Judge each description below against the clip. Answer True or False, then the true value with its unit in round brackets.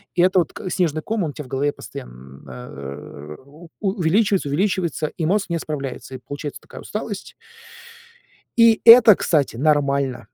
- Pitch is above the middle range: False (155 Hz)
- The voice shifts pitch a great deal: True (6.1 semitones)